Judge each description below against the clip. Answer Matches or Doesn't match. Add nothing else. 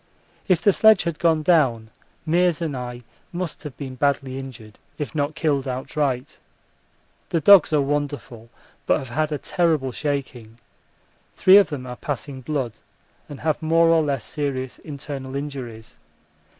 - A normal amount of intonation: Matches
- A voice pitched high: Doesn't match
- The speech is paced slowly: Doesn't match